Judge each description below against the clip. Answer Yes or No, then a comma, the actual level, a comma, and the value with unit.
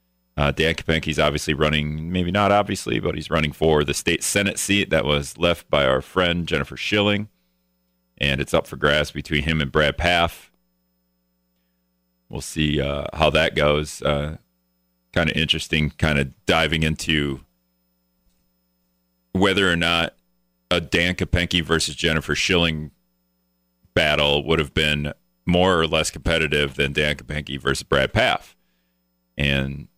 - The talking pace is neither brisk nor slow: Yes, average, 145 wpm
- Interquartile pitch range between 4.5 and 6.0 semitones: Yes, wide, 5.6 semitones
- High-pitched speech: No, very low, 75 Hz